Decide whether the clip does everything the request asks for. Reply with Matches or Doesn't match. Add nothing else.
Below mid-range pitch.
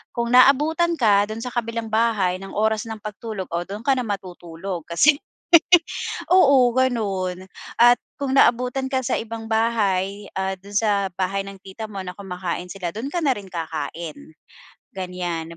Doesn't match